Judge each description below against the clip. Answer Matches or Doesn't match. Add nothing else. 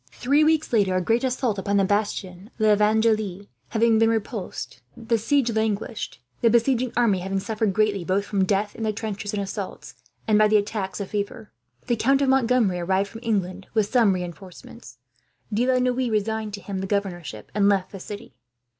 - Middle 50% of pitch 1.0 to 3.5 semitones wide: Matches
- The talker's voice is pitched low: Doesn't match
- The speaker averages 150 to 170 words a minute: Doesn't match